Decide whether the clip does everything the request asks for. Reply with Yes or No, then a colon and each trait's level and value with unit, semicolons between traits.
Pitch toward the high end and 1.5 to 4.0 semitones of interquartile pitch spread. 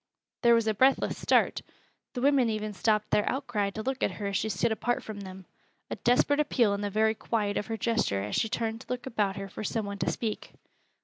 Yes: high, 220 Hz; average, 2.8 semitones